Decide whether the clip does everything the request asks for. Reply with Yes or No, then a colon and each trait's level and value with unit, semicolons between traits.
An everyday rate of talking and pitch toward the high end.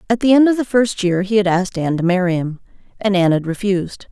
No: fast, 265 wpm; high, 195 Hz